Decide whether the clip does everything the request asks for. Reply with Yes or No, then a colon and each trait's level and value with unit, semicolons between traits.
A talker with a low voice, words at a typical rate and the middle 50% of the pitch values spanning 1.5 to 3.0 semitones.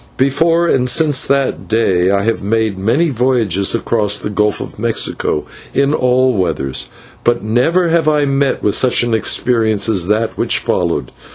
No: low, 115 Hz; average, 165 wpm; average, 4.7 semitones